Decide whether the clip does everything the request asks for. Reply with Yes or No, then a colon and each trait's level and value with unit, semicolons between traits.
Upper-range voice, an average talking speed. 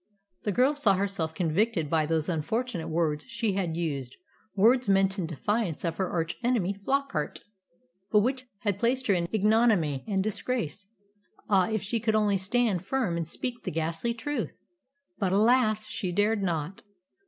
Yes: high, 200 Hz; average, 165 wpm